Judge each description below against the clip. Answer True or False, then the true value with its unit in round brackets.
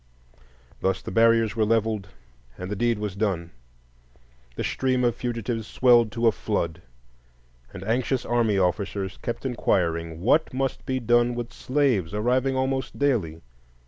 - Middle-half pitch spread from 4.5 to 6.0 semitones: False (3.9 semitones)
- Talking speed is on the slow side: False (145 wpm)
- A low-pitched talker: True (115 Hz)